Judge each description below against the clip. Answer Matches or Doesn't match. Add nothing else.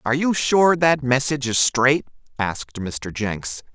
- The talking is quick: Doesn't match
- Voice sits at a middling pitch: Doesn't match